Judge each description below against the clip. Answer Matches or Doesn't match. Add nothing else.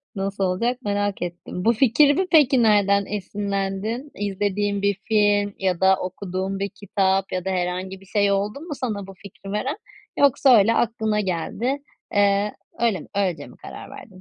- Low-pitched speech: Doesn't match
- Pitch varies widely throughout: Doesn't match